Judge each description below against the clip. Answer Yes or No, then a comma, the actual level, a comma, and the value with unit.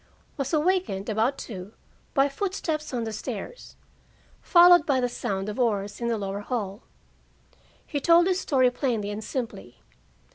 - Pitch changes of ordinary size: No, wide, 6.7 semitones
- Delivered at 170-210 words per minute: No, average, 150 wpm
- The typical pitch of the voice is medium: No, high, 245 Hz